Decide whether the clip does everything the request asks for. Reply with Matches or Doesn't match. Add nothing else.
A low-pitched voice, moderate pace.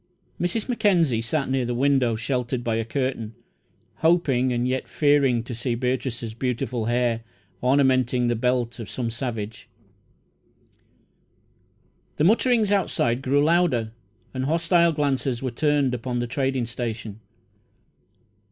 Doesn't match